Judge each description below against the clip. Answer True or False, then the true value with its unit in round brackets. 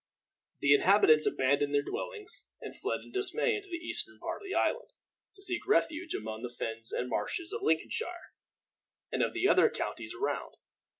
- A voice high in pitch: True (345 Hz)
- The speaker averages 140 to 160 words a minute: False (175 wpm)